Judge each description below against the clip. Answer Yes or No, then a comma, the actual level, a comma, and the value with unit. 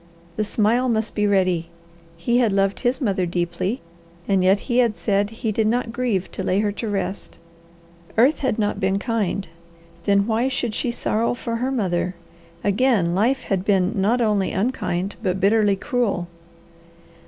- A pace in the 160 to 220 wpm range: Yes, average, 165 wpm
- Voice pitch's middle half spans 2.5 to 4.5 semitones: Yes, average, 3.5 semitones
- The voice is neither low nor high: No, high, 210 Hz